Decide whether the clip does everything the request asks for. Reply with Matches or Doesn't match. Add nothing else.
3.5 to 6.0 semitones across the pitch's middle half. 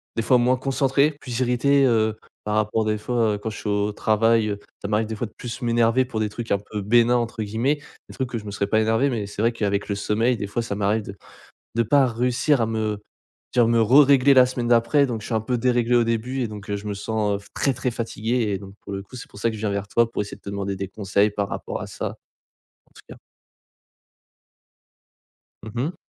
Doesn't match